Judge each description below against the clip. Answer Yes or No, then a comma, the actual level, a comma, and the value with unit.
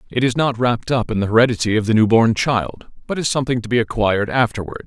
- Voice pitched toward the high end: No, low, 115 Hz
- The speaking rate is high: Yes, fast, 245 wpm